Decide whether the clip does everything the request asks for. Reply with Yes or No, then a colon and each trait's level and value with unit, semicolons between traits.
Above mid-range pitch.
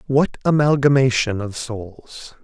No: low, 125 Hz